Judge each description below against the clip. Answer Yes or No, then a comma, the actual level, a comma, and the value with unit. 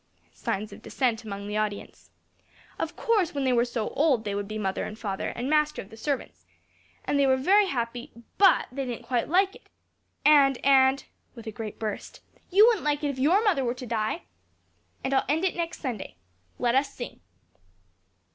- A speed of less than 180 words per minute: No, average, 195 wpm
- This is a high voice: Yes, very high, 260 Hz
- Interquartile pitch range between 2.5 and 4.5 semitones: No, average, 5.2 semitones